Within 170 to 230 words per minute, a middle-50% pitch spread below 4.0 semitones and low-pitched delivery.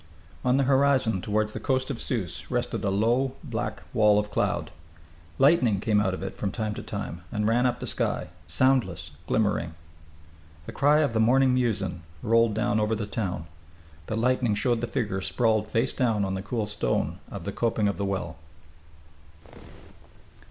Yes: average, 175 wpm; average, 3.5 semitones; low, 110 Hz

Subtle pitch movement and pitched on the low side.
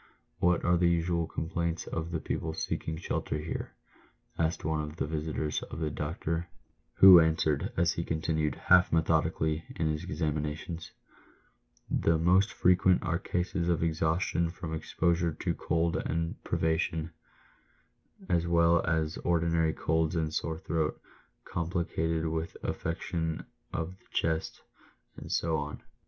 Yes: narrow, 1.3 semitones; very low, 80 Hz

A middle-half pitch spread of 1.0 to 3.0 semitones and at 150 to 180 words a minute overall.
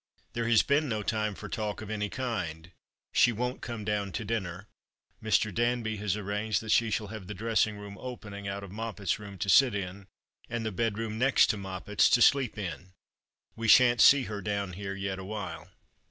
No: narrow, 2.4 semitones; average, 195 wpm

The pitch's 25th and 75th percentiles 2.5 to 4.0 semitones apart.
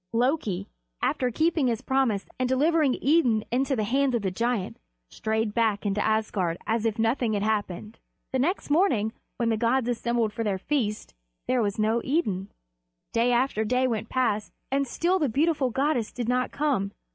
Yes: average, 3.7 semitones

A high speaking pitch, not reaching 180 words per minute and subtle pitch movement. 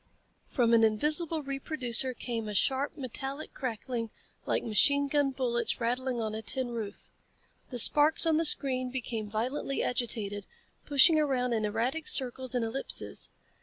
No: very high, 255 Hz; average, 145 wpm; average, 3.3 semitones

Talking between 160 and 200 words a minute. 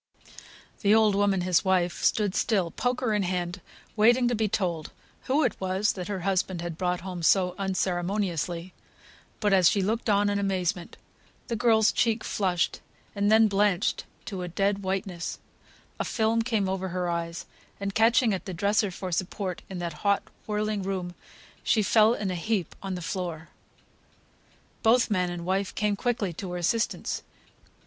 Yes: average, 165 wpm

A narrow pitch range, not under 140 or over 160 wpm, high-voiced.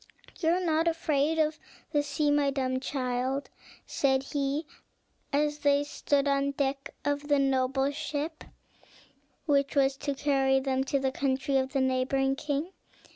Yes: narrow, 1.5 semitones; average, 155 wpm; very high, 280 Hz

